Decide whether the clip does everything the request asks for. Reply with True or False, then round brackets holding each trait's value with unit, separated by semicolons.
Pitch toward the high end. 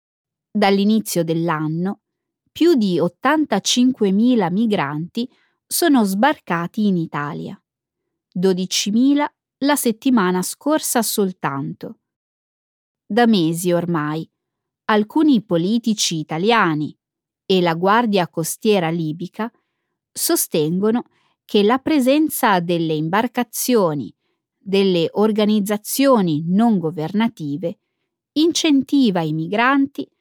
True (210 Hz)